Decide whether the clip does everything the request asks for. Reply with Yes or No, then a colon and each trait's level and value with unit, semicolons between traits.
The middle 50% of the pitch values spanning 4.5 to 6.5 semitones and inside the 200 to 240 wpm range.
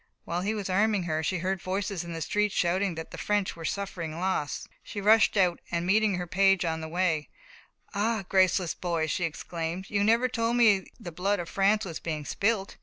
No: average, 3.3 semitones; fast, 205 wpm